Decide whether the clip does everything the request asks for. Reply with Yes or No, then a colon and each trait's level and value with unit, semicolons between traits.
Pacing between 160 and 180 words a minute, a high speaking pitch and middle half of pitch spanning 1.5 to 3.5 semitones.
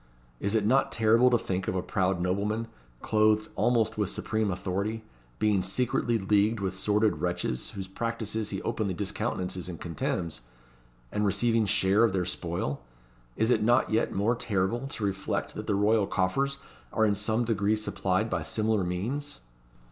No: average, 165 wpm; low, 105 Hz; average, 2.9 semitones